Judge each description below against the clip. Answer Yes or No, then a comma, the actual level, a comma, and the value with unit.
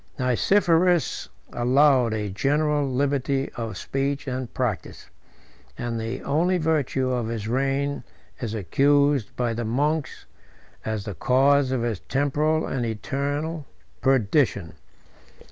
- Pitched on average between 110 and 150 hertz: Yes, low, 135 Hz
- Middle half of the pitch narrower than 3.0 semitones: No, average, 3.6 semitones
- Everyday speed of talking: No, slow, 115 wpm